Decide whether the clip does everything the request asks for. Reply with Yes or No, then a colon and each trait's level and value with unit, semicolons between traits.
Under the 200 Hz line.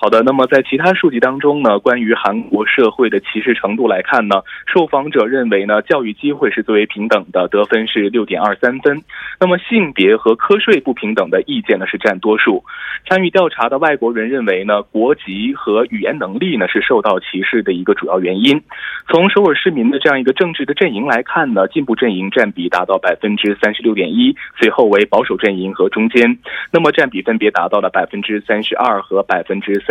Yes: medium, 140 Hz